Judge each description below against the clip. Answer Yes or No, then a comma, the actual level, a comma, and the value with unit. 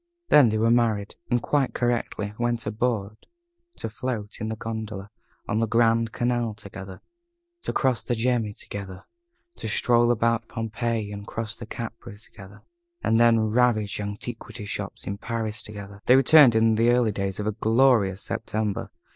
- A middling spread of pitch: No, narrow, 2.2 semitones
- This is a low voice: Yes, low, 110 Hz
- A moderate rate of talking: Yes, average, 160 wpm